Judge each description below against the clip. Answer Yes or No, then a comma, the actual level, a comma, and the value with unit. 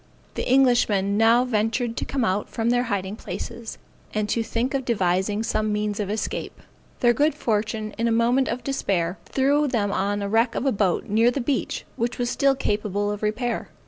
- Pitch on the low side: No, high, 225 Hz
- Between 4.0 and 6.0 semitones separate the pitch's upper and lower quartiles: No, average, 3.0 semitones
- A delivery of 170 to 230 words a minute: Yes, average, 195 wpm